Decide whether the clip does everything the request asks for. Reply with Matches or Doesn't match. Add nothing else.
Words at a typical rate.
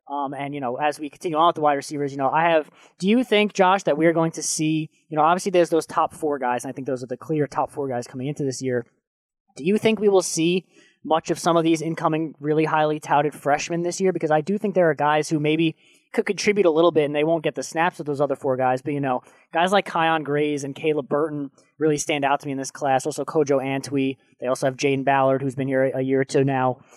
Doesn't match